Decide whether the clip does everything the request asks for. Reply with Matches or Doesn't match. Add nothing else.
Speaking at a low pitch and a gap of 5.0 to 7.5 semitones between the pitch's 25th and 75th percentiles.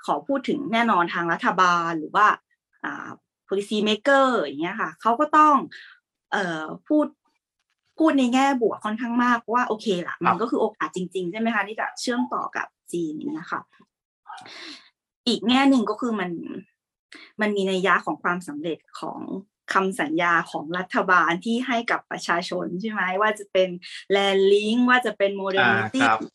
Doesn't match